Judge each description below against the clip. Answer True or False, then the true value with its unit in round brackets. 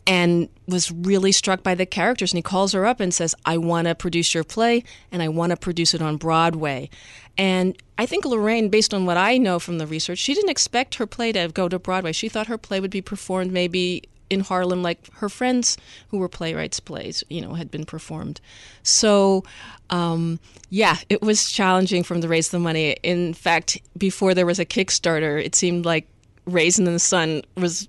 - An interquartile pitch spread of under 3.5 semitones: True (2.7 semitones)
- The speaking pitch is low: False (180 Hz)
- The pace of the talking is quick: True (210 wpm)